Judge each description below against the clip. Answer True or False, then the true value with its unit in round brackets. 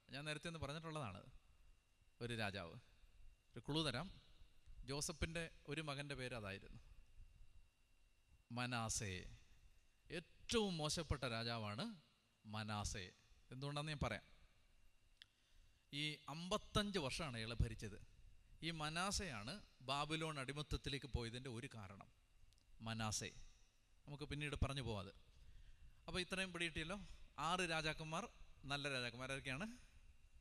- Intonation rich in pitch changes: True (7.0 semitones)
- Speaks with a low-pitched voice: True (120 Hz)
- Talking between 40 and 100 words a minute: True (90 wpm)